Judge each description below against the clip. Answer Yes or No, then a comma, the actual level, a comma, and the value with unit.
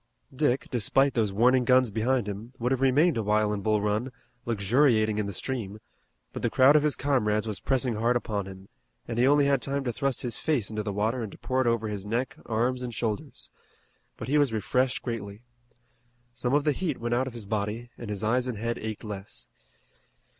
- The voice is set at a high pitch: No, low, 115 Hz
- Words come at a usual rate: No, fast, 215 wpm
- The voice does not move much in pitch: No, average, 3.5 semitones